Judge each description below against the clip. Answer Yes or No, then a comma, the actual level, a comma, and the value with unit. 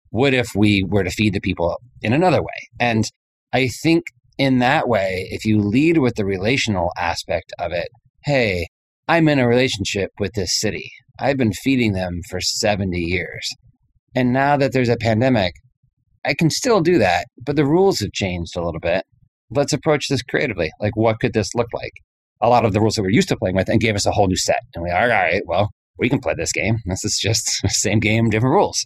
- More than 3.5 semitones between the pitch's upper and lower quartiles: Yes, average, 4.4 semitones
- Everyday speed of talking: No, fast, 220 wpm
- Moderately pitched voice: No, low, 110 Hz